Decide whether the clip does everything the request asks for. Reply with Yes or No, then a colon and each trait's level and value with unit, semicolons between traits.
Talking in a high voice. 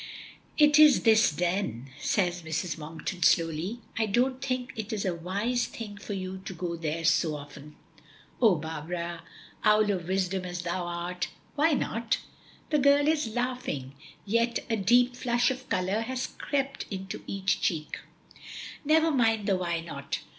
Yes: high, 195 Hz